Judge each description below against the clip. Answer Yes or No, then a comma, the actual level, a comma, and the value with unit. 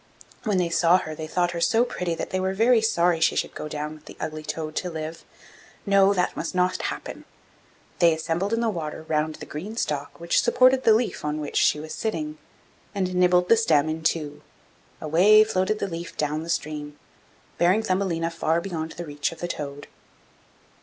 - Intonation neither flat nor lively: Yes, average, 3.9 semitones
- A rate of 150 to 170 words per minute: No, average, 200 wpm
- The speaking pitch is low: No, medium, 170 Hz